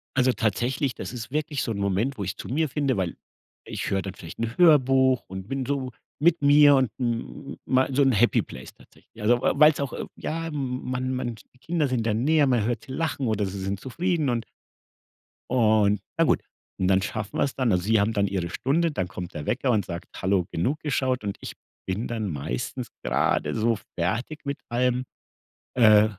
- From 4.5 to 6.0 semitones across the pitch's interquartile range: Yes, average, 5.1 semitones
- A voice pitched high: No, low, 120 Hz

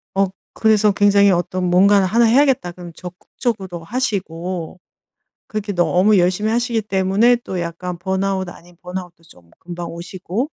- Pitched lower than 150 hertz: No, high, 190 Hz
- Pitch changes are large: No, average, 3.1 semitones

